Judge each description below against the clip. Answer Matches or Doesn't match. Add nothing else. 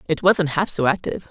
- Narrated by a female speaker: Matches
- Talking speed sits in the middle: Doesn't match